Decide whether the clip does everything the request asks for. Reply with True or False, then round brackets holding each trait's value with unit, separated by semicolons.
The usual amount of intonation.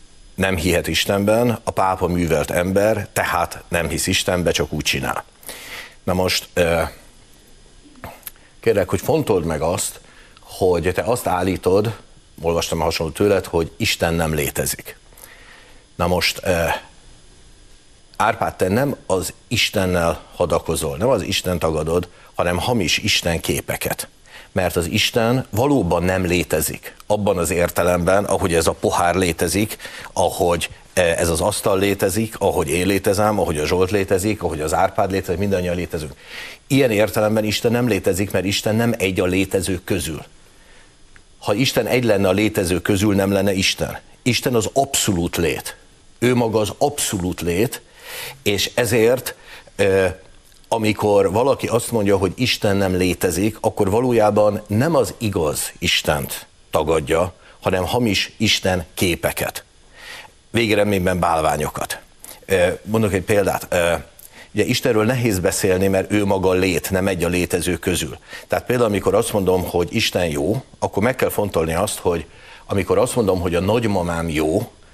True (3.1 semitones)